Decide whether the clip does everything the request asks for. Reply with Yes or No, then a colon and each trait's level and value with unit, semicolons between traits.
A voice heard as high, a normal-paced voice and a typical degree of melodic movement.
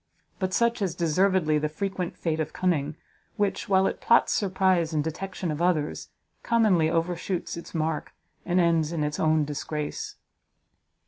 No: medium, 170 Hz; average, 150 wpm; average, 3.3 semitones